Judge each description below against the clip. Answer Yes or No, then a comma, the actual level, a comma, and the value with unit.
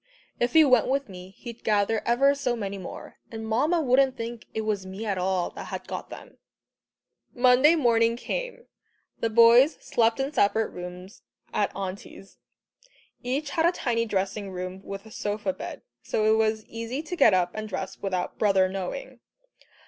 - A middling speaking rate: Yes, average, 170 wpm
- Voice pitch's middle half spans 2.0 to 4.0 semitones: No, average, 4.6 semitones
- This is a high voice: Yes, high, 225 Hz